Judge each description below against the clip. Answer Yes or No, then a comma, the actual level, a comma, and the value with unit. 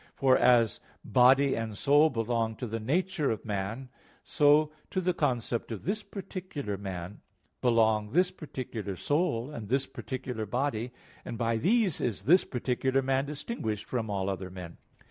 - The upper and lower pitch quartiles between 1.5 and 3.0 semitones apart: No, average, 4.9 semitones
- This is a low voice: Yes, low, 125 Hz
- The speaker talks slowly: No, average, 155 wpm